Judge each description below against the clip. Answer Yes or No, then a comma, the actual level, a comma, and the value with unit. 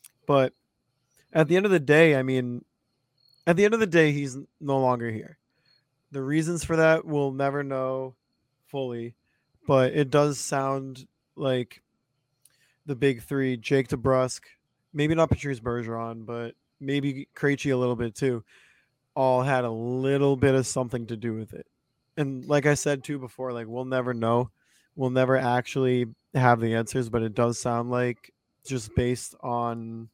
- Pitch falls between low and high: No, low, 130 Hz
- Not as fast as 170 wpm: Yes, average, 160 wpm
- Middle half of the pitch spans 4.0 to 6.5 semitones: No, narrow, 2.6 semitones